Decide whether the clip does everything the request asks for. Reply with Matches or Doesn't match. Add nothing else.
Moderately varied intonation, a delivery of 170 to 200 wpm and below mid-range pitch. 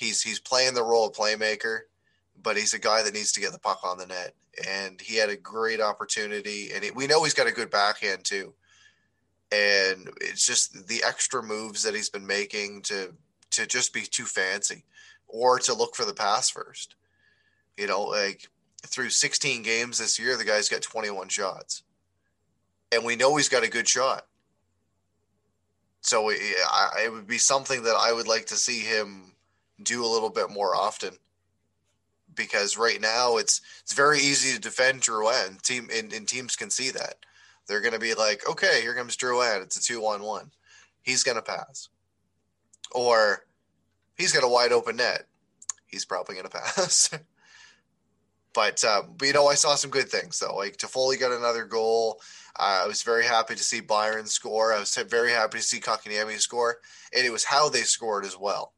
Matches